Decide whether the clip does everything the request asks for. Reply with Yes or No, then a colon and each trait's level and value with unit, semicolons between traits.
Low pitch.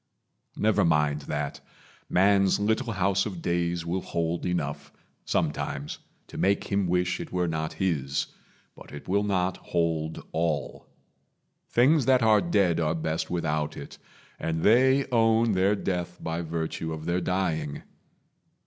Yes: very low, 90 Hz